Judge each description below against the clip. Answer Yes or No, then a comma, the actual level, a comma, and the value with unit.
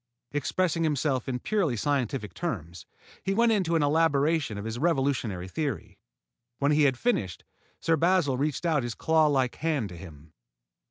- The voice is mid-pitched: Yes, medium, 145 Hz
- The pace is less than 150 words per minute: No, average, 155 wpm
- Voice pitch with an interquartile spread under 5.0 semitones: No, wide, 5.4 semitones